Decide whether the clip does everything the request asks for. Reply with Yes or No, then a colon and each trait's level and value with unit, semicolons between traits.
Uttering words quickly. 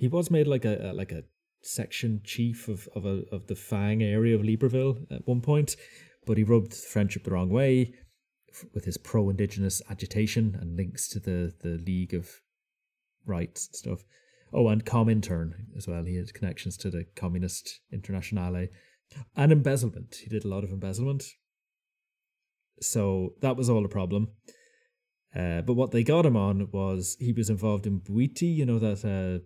No: average, 175 wpm